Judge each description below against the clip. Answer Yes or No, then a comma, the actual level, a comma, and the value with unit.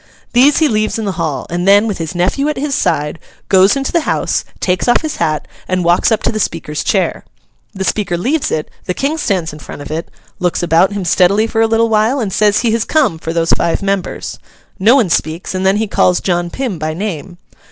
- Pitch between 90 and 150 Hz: No, high, 195 Hz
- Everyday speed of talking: No, fast, 230 wpm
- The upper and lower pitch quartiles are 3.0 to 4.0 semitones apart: No, average, 4.7 semitones